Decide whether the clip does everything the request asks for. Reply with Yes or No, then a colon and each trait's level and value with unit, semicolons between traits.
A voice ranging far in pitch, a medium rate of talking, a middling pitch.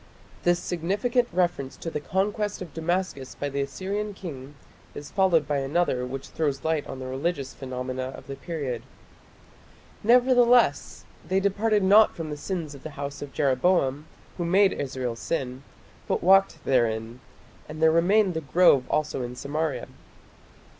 Yes: wide, 5.7 semitones; average, 155 wpm; medium, 155 Hz